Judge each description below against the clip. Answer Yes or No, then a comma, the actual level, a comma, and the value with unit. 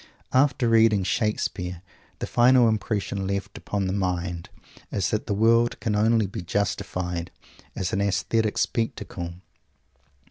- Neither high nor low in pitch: No, low, 100 Hz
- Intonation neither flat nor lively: Yes, average, 3.4 semitones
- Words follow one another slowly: Yes, slow, 130 wpm